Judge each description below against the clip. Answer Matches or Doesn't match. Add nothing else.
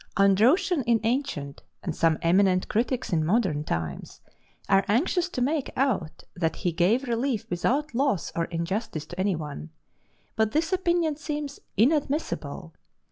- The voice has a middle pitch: Doesn't match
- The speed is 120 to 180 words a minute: Matches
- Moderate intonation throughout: Doesn't match